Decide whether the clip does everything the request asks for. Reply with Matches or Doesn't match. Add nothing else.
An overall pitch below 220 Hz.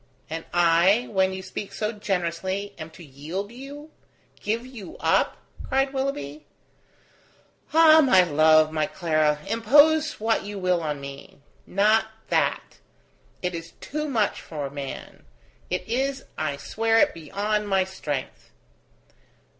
Matches